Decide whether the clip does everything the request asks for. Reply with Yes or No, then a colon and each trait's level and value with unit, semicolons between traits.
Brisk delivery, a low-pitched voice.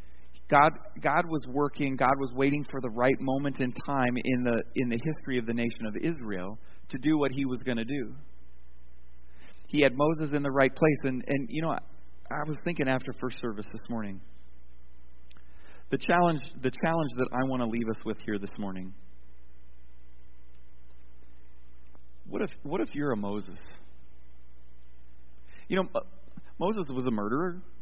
No: average, 170 wpm; low, 115 Hz